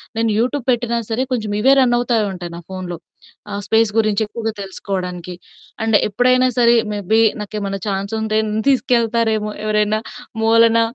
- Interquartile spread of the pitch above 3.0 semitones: No, narrow, 2.5 semitones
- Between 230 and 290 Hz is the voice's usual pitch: No, high, 220 Hz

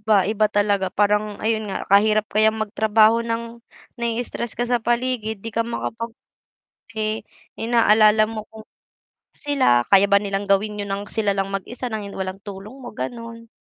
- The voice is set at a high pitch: Yes, high, 215 Hz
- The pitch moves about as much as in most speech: No, narrow, 2.1 semitones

